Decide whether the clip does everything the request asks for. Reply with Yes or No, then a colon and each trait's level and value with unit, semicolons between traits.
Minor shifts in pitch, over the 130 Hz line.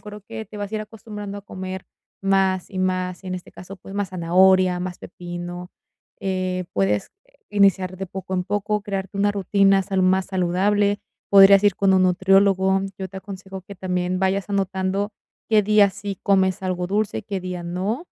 Yes: narrow, 1.5 semitones; high, 190 Hz